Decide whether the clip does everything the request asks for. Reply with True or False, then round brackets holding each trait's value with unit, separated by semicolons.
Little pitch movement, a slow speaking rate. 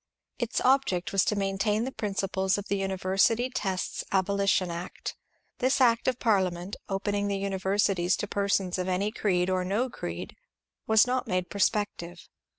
False (2.3 semitones; 155 wpm)